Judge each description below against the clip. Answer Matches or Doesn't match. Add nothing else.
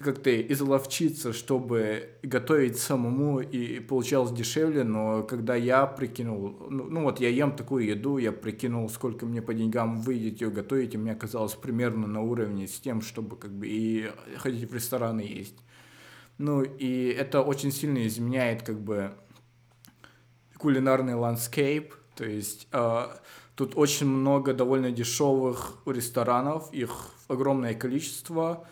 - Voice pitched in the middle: Doesn't match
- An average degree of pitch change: Matches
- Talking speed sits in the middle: Matches